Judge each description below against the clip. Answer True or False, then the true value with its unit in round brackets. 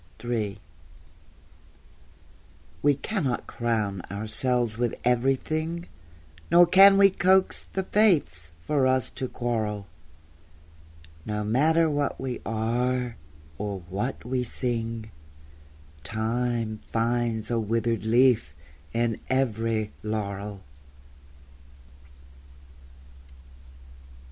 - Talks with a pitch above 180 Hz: False (120 Hz)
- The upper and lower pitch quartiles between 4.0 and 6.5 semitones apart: False (3.4 semitones)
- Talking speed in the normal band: False (85 wpm)